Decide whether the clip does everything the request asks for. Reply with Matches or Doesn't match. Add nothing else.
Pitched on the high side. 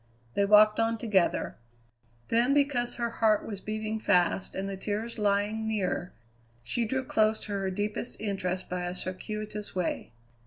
Matches